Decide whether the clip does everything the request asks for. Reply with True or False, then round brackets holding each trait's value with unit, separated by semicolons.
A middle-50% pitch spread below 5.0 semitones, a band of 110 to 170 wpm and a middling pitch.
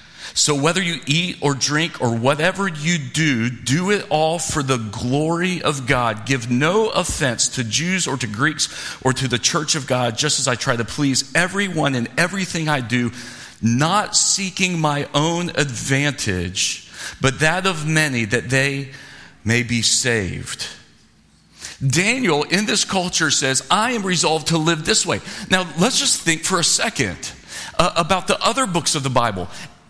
False (5.4 semitones; 165 wpm; 150 Hz)